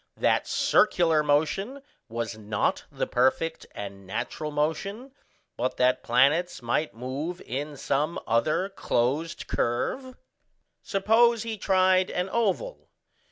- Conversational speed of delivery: No, slow, 115 wpm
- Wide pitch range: Yes, wide, 7.4 semitones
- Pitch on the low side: No, medium, 155 Hz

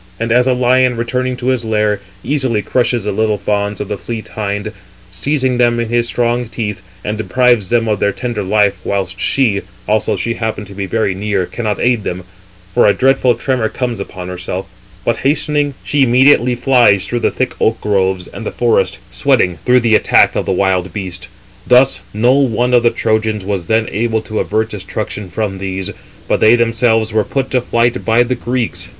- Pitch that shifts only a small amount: No, average, 3.3 semitones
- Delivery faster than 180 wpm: Yes, average, 195 wpm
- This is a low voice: Yes, low, 110 Hz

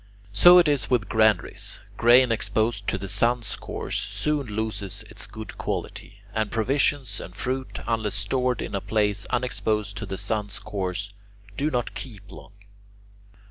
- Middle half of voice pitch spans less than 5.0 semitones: Yes, average, 3.7 semitones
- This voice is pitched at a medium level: No, low, 110 Hz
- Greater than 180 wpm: No, average, 150 wpm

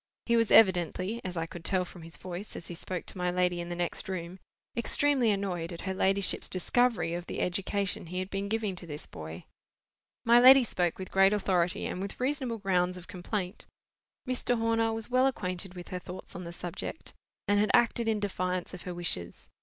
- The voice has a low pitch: No, medium, 185 Hz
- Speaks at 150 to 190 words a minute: No, average, 200 wpm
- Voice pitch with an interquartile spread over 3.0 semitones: Yes, average, 3.7 semitones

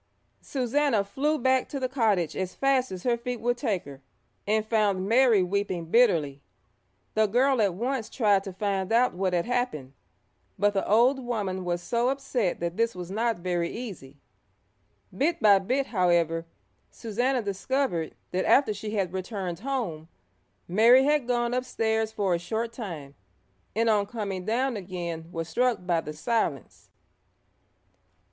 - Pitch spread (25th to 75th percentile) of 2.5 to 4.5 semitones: No, average, 5.2 semitones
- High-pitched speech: Yes, high, 215 Hz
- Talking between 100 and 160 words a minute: Yes, average, 155 wpm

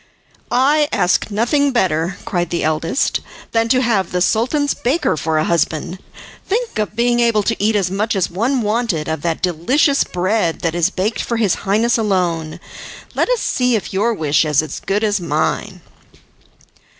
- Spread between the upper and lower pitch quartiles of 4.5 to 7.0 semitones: Yes, wide, 5.6 semitones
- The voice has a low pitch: No, high, 205 Hz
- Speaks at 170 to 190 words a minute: Yes, average, 175 wpm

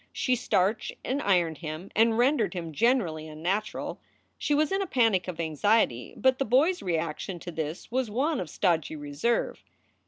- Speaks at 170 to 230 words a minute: Yes, average, 175 wpm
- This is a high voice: Yes, high, 195 Hz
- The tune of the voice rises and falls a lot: Yes, wide, 7.6 semitones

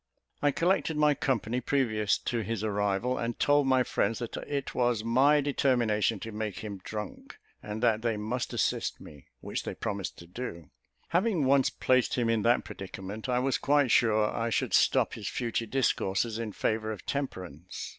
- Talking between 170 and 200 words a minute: Yes, average, 175 wpm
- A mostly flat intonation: No, average, 3.7 semitones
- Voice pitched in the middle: No, low, 115 Hz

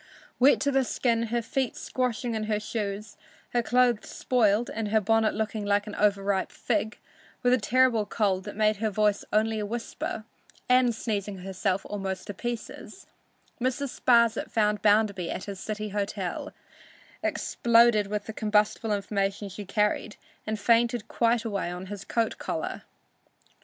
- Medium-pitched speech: No, high, 215 Hz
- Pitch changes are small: Yes, narrow, 2.3 semitones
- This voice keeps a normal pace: Yes, average, 155 wpm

